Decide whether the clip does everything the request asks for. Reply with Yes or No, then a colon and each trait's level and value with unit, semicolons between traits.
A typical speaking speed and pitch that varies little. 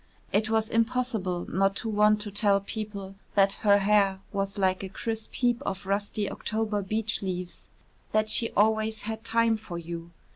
Yes: average, 170 wpm; narrow, 2.1 semitones